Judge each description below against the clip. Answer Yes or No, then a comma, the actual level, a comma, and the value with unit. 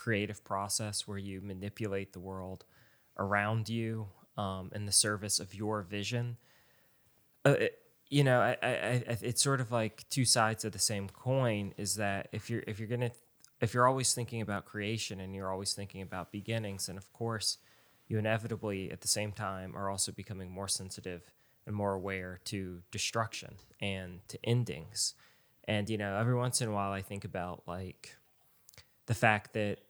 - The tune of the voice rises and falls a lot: No, average, 2.8 semitones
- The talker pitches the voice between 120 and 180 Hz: No, low, 105 Hz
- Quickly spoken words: No, average, 180 wpm